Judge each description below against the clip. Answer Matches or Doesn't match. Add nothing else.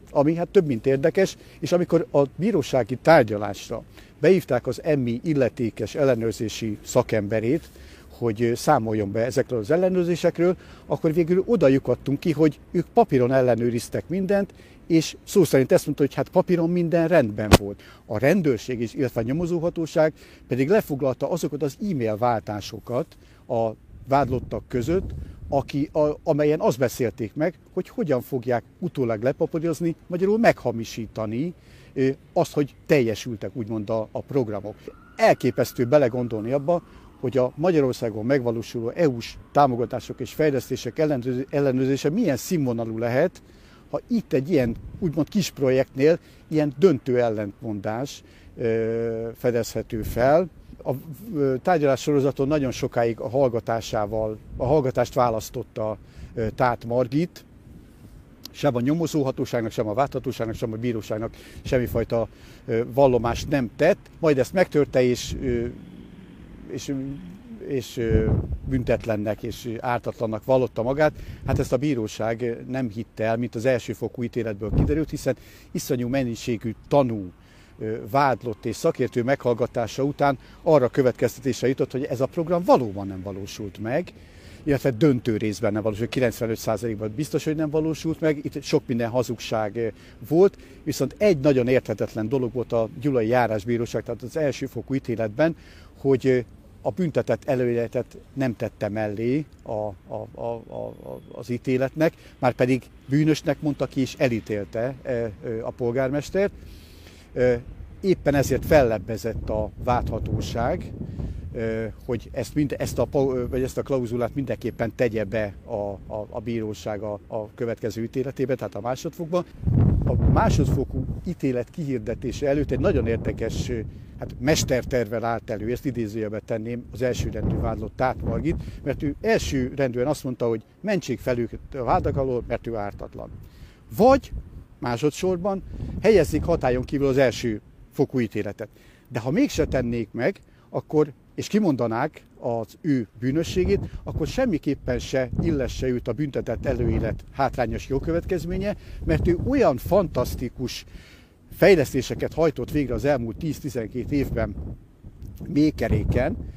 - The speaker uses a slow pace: Doesn't match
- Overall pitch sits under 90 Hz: Doesn't match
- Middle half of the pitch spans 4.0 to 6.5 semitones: Matches